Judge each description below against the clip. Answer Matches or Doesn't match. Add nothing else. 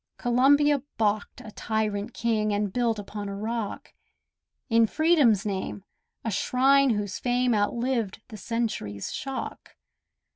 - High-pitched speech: Matches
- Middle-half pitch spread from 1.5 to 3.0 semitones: Doesn't match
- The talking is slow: Matches